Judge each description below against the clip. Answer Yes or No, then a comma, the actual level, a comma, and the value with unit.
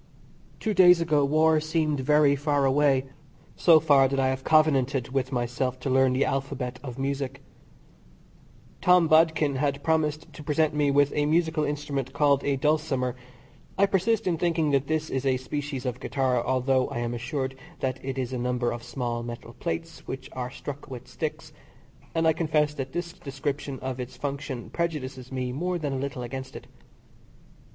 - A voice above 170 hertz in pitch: No, medium, 140 Hz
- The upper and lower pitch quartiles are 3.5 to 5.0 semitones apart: No, average, 2.8 semitones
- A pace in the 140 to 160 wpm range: No, average, 175 wpm